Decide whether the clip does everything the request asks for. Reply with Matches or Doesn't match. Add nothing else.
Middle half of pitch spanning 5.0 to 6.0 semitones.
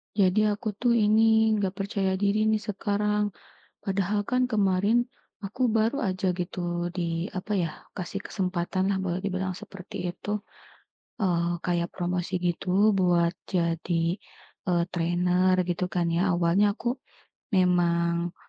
Doesn't match